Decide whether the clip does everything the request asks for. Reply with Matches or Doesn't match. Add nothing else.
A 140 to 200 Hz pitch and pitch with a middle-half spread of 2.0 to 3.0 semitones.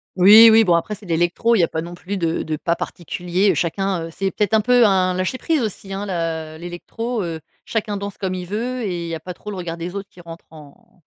Doesn't match